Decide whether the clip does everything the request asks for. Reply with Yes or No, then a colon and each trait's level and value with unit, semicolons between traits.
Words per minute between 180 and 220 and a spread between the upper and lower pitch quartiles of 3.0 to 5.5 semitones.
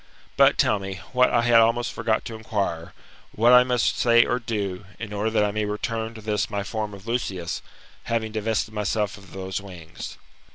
No: average, 195 wpm; narrow, 2.5 semitones